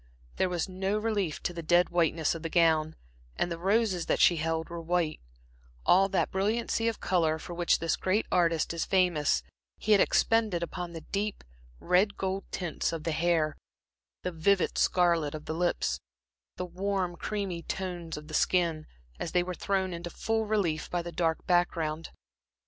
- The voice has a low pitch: No, medium, 175 Hz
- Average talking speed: Yes, average, 175 wpm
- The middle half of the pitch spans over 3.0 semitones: No, narrow, 2.6 semitones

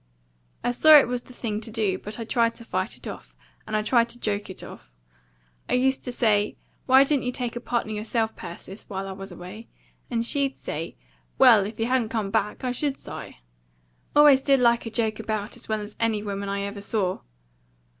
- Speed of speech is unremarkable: No, fast, 215 wpm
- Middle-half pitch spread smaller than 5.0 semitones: Yes, average, 3.0 semitones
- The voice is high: Yes, high, 225 Hz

